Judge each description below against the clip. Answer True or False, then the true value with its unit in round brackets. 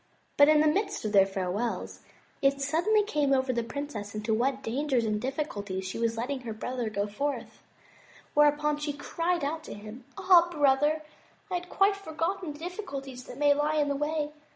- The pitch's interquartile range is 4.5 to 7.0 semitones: True (4.9 semitones)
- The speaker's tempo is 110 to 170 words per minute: False (185 wpm)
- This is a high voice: True (285 Hz)